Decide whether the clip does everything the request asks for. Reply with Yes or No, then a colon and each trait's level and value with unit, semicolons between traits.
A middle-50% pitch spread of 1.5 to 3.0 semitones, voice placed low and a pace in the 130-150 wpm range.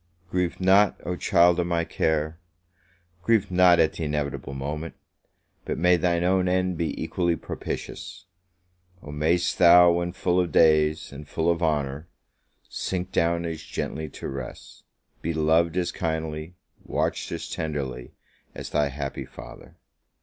Yes: narrow, 2.6 semitones; very low, 85 Hz; average, 145 wpm